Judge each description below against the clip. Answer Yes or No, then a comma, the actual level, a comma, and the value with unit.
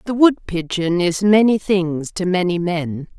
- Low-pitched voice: No, medium, 185 Hz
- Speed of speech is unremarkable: Yes, average, 150 wpm